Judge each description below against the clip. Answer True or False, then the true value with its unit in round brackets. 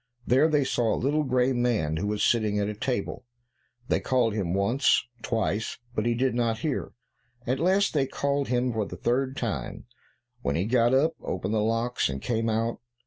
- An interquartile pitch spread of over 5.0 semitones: False (3.4 semitones)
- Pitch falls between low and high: False (120 Hz)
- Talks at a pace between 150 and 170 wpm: False (195 wpm)